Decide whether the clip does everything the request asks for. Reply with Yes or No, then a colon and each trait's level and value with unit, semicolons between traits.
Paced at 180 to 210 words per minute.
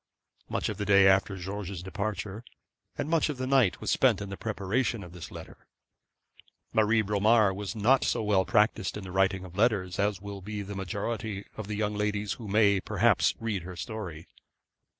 Yes: average, 190 wpm